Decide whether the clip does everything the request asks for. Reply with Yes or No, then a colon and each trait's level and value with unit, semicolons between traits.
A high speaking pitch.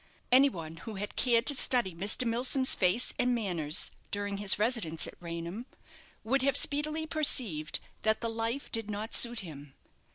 Yes: high, 225 Hz